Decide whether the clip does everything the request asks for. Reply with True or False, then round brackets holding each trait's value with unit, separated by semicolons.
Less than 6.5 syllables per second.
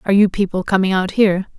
False (7.0 syllables/s)